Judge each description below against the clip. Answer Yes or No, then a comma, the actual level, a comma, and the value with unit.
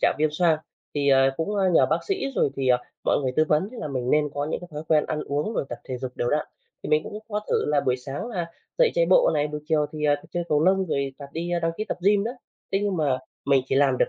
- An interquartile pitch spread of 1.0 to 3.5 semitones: No, average, 4.3 semitones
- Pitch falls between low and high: Yes, medium, 150 Hz